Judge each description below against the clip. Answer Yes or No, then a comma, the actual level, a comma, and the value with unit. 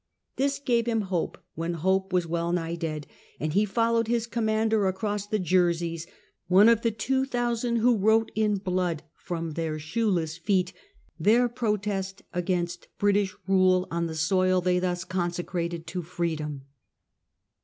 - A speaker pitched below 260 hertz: Yes, medium, 185 Hz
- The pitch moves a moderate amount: Yes, average, 4.2 semitones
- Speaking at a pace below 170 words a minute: Yes, average, 150 wpm